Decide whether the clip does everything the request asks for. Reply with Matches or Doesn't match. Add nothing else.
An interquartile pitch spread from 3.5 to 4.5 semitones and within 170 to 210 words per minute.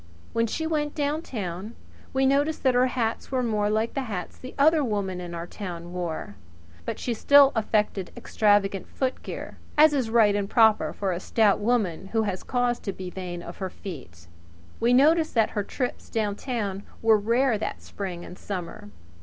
Doesn't match